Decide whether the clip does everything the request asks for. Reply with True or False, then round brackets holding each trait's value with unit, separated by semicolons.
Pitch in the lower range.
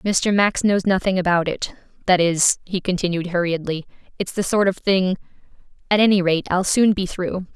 False (185 Hz)